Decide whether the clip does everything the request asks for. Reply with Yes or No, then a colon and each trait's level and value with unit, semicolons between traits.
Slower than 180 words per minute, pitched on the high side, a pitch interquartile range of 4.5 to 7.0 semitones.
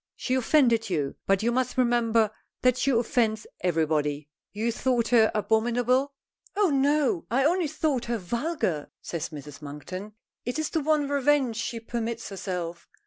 Yes: average, 150 wpm; high, 235 Hz; wide, 5.6 semitones